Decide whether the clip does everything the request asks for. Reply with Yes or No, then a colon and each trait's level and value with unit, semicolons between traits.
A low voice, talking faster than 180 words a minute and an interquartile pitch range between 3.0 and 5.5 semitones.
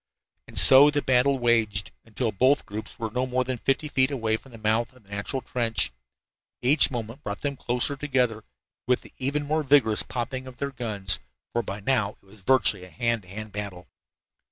Yes: low, 120 Hz; average, 200 wpm; average, 3.6 semitones